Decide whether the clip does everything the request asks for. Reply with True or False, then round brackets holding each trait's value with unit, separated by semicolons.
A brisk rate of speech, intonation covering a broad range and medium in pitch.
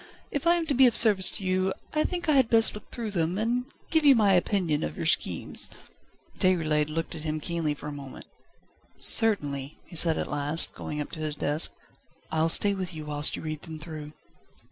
True (210 wpm; 6.3 semitones; 170 Hz)